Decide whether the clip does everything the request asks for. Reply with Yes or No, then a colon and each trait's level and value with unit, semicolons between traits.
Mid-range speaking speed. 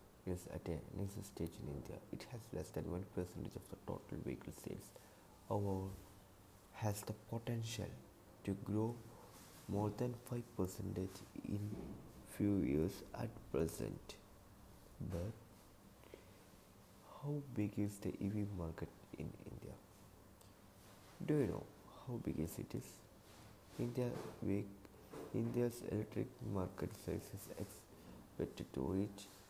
No: slow, 120 wpm